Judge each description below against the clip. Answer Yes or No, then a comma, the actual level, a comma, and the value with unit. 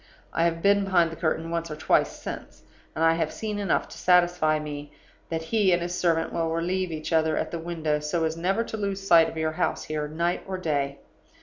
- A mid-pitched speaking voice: Yes, medium, 165 Hz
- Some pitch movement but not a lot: No, narrow, 2.1 semitones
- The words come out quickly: Yes, fast, 225 wpm